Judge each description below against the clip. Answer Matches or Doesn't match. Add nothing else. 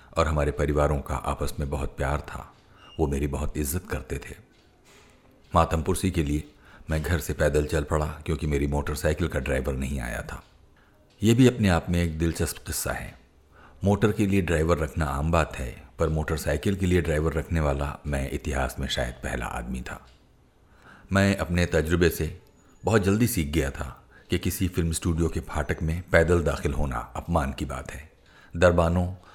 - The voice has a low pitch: Matches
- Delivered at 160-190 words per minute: Matches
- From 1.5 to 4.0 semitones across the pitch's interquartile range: Matches